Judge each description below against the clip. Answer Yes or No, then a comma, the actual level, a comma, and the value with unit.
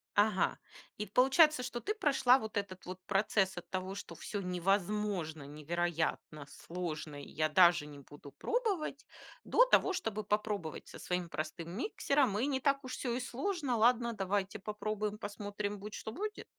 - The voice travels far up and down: Yes, wide, 5.9 semitones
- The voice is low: No, high, 205 Hz